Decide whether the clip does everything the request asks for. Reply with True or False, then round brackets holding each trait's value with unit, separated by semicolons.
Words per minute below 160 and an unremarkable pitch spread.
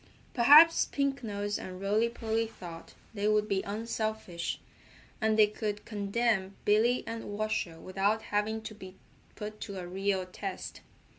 False (145 wpm; 2.1 semitones)